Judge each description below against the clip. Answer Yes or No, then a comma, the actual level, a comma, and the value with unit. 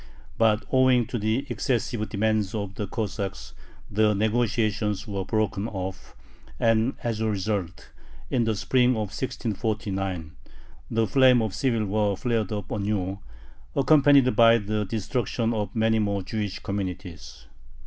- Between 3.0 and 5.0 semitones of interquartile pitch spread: No, narrow, 2.5 semitones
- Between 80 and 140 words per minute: Yes, slow, 135 wpm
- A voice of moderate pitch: No, low, 110 Hz